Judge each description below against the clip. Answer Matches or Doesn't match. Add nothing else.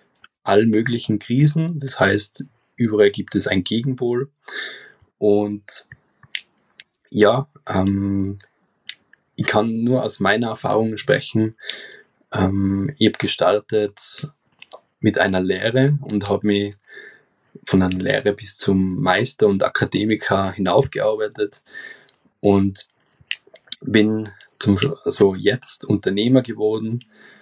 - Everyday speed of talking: Doesn't match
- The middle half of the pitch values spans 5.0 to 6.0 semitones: Doesn't match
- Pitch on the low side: Matches